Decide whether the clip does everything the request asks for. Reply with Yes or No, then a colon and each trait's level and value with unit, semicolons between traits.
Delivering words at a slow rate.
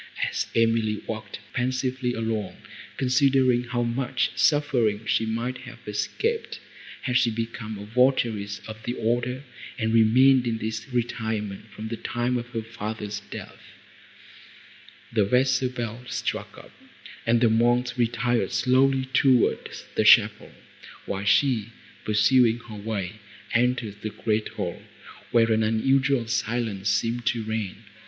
Yes: slow, 130 wpm